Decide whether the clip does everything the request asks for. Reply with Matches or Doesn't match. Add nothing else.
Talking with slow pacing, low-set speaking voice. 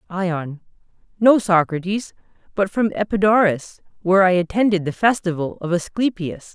Doesn't match